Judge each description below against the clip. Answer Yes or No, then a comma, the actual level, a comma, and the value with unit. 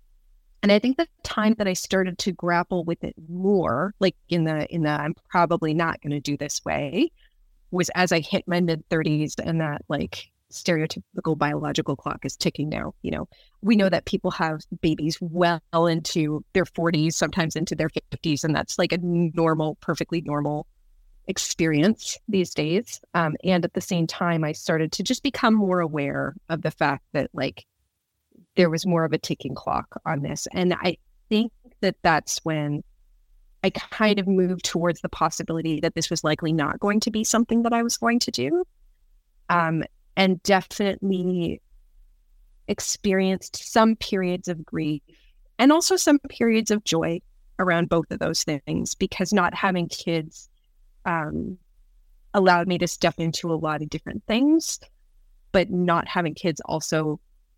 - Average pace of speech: Yes, average, 170 wpm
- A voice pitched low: No, medium, 175 Hz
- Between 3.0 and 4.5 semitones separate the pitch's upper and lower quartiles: Yes, average, 3.4 semitones